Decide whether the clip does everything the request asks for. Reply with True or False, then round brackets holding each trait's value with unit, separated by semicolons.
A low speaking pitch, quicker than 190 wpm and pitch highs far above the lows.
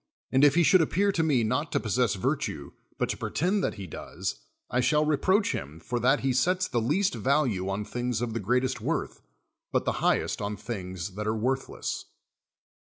True (125 Hz; 200 wpm; 6.2 semitones)